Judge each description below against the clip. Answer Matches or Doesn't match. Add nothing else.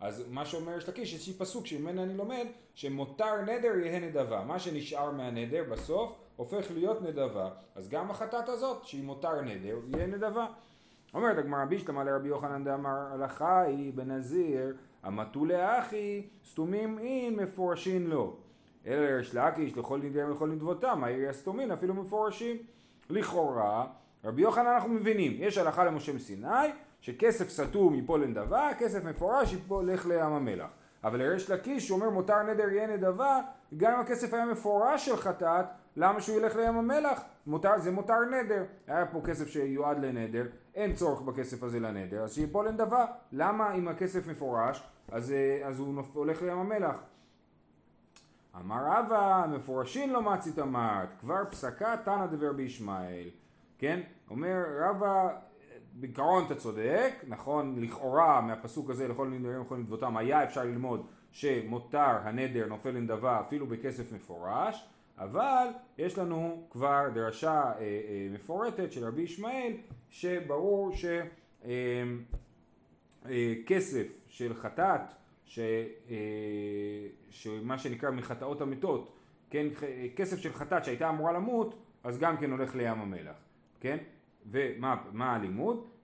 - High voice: Doesn't match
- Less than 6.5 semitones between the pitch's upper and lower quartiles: Doesn't match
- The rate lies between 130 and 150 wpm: Matches